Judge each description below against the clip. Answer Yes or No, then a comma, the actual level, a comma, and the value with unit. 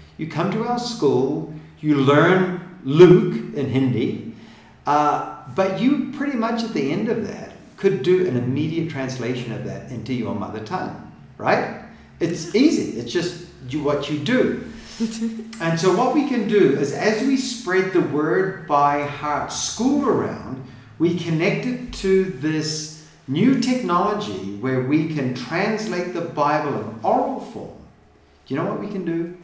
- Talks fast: No, average, 160 wpm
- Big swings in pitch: Yes, wide, 6.3 semitones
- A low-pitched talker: No, medium, 170 Hz